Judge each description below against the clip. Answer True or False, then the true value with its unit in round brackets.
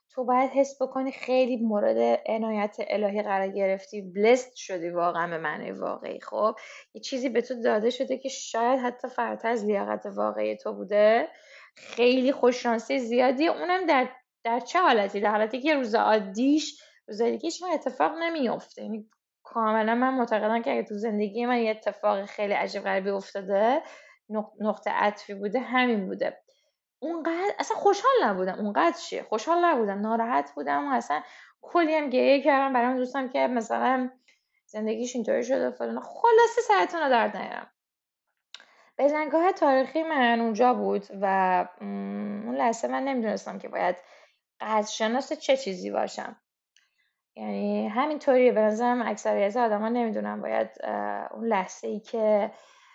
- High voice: True (235 Hz)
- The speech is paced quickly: False (145 wpm)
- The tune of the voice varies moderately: True (4.5 semitones)